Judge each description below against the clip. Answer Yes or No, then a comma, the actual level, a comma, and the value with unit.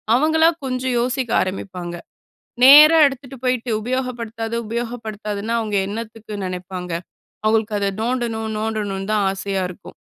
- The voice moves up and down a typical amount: Yes, average, 3.7 semitones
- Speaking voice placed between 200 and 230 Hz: Yes, high, 225 Hz